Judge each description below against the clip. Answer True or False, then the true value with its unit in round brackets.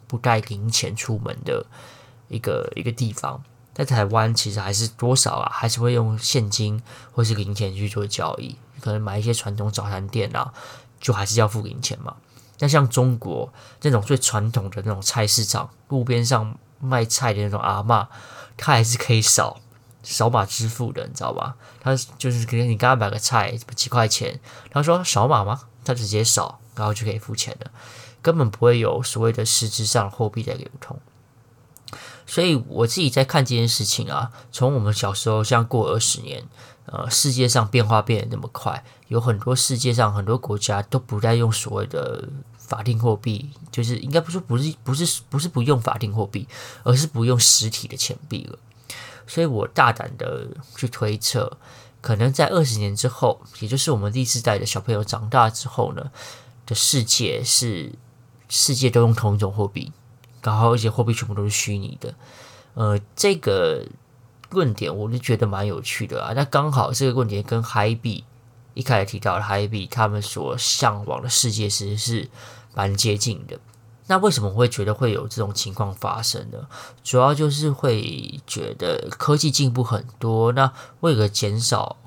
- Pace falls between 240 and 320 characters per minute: True (270 characters per minute)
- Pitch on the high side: False (120 Hz)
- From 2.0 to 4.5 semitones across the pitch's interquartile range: True (2.7 semitones)